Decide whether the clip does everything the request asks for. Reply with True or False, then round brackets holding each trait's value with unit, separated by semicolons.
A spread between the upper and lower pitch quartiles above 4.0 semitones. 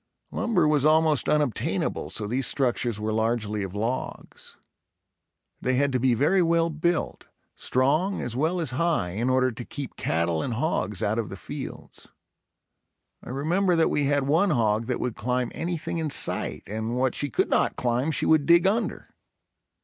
True (5.5 semitones)